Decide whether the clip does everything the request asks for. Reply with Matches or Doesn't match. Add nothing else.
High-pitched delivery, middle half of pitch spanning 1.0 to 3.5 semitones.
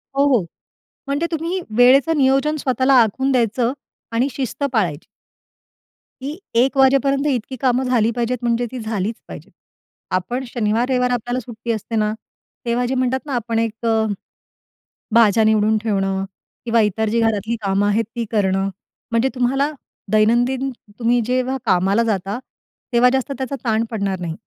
Matches